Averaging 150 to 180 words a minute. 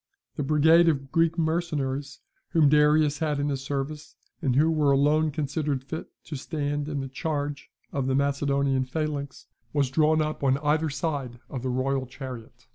Yes: average, 170 wpm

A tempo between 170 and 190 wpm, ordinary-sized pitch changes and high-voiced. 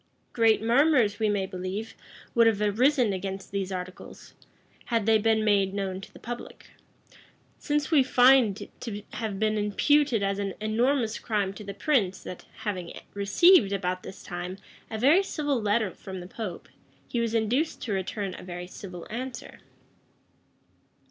No: average, 160 wpm; average, 3.6 semitones; high, 210 Hz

